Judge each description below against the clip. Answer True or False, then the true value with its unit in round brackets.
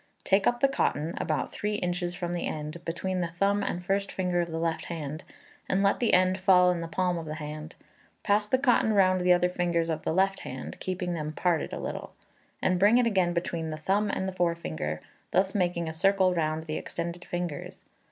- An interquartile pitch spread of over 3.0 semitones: False (2.5 semitones)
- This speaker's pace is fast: True (210 wpm)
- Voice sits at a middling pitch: True (175 Hz)